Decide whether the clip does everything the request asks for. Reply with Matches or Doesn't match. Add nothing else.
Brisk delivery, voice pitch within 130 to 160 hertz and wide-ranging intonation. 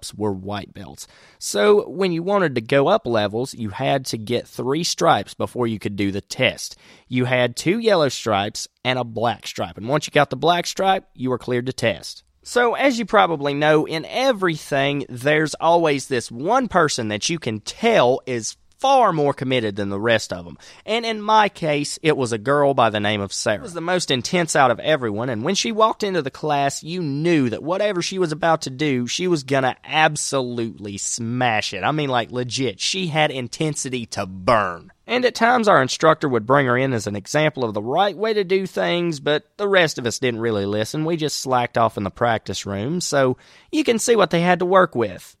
Matches